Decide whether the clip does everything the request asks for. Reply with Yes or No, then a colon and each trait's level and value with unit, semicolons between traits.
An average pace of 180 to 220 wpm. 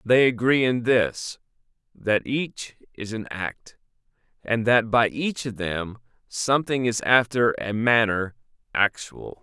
No: slow, 135 wpm